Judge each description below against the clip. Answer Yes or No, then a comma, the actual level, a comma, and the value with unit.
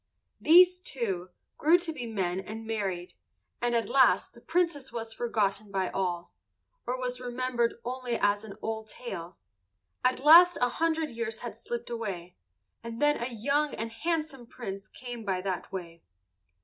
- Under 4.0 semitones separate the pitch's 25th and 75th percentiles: No, average, 4.4 semitones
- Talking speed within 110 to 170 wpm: Yes, average, 160 wpm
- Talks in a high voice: Yes, high, 235 Hz